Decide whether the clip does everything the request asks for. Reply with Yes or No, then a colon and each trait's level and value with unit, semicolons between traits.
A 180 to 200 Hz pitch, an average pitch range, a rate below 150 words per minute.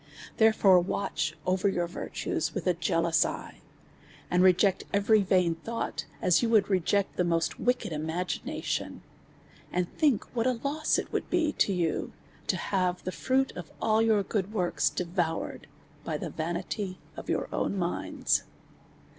No: medium, 185 Hz; average, 3.9 semitones; average, 155 wpm